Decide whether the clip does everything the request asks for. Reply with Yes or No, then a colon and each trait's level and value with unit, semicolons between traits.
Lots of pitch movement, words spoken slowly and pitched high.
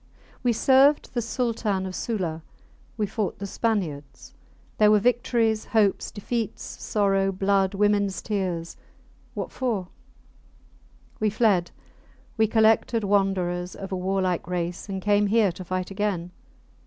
No: average, 2.9 semitones; slow, 130 wpm; high, 200 Hz